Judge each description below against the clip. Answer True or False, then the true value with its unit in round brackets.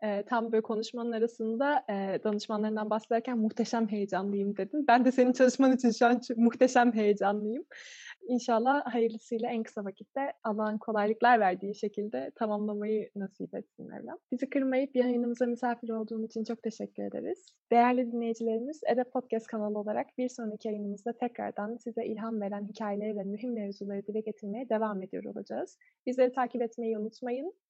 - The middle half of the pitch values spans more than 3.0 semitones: False (2.5 semitones)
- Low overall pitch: False (230 Hz)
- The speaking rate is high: True (145 wpm)